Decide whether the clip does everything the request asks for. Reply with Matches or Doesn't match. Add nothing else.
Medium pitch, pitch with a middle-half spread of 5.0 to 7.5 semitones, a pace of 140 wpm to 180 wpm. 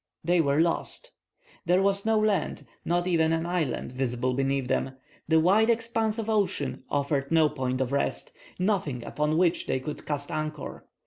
Matches